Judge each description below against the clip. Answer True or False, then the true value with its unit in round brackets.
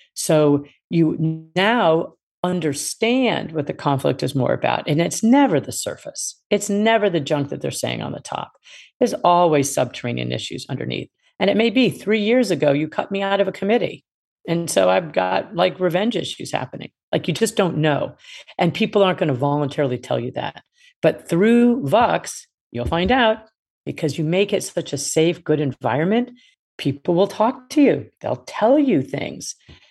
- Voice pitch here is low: False (180 Hz)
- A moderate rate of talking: True (180 wpm)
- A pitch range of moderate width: False (6.6 semitones)